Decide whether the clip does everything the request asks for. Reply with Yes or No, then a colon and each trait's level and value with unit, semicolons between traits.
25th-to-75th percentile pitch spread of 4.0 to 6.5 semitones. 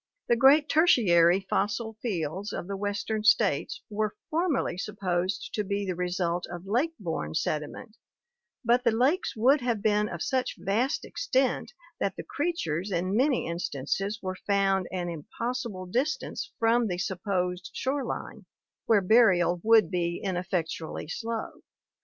Yes: average, 4.9 semitones